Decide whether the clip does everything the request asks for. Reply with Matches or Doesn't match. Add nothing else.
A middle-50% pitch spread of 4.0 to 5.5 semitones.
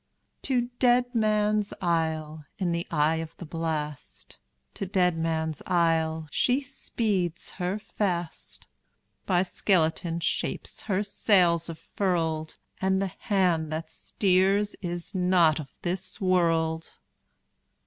Doesn't match